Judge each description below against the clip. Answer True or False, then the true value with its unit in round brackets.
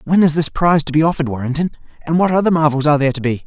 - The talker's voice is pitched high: False (155 Hz)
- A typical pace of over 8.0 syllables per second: True (8.2 syllables/s)